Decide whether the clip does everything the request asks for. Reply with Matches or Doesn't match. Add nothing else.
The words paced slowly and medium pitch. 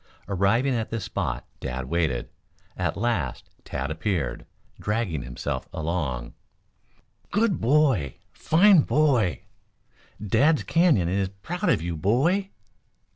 Doesn't match